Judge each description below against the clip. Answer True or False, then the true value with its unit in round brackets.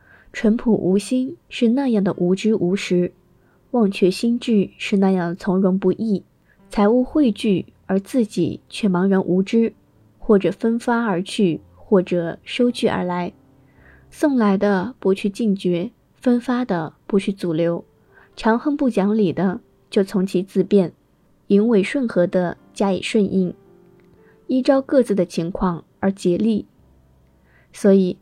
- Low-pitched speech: False (195 Hz)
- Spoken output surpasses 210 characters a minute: False (200 characters per minute)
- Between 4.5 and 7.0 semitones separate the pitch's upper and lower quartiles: False (3.8 semitones)